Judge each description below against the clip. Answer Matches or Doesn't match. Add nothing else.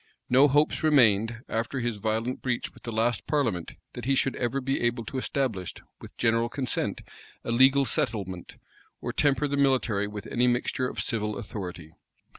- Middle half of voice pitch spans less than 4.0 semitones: Matches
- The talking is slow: Doesn't match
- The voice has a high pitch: Doesn't match